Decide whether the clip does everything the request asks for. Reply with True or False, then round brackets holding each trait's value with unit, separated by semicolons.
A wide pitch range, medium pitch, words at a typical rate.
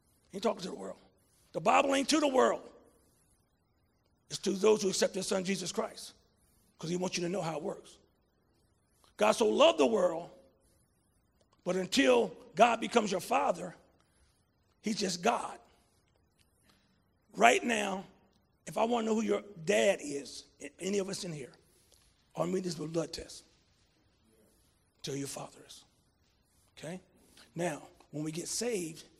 True (8.0 semitones; 175 Hz; 155 wpm)